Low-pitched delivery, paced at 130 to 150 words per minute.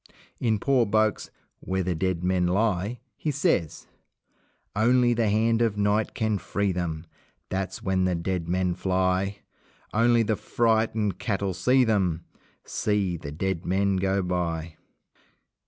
Yes: very low, 95 Hz; average, 140 wpm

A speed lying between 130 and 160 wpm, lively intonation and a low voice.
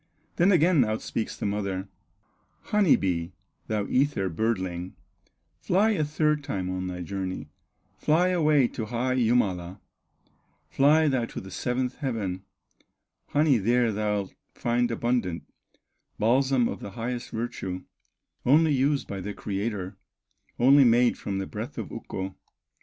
Yes: slow, 135 wpm; wide, 6.1 semitones; low, 115 Hz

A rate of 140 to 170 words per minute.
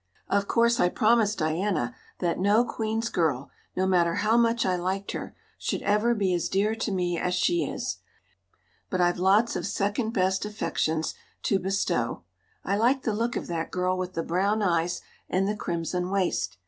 No: average, 180 wpm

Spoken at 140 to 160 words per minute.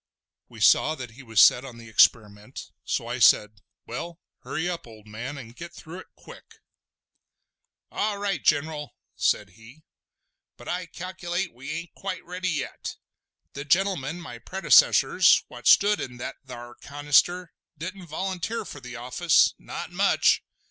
Yes: average, 150 wpm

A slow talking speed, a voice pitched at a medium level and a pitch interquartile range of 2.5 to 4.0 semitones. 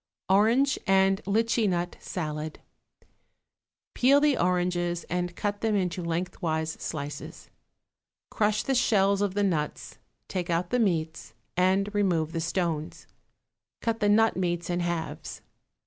Yes: slow, 130 wpm; medium, 180 Hz; average, 3.4 semitones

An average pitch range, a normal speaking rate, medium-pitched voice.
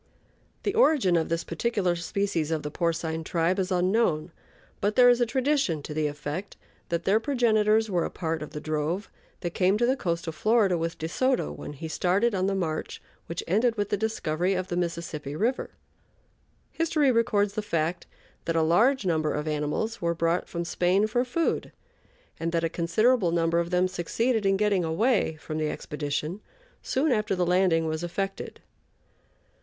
Yes: average, 4.8 semitones; average, 180 wpm; medium, 180 Hz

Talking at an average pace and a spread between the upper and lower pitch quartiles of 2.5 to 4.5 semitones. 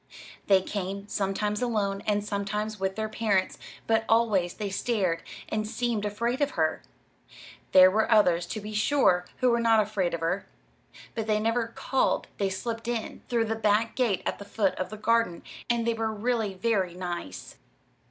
Yes: average, 175 wpm; average, 2.9 semitones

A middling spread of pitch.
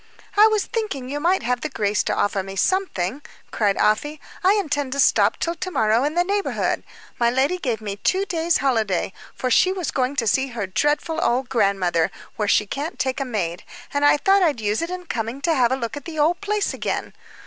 No: wide, 7.4 semitones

